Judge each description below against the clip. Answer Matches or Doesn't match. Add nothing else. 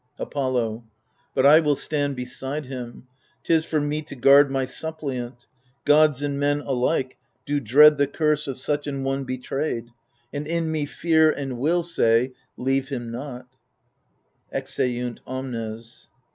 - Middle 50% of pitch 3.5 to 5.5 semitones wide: Doesn't match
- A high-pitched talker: Doesn't match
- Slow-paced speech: Doesn't match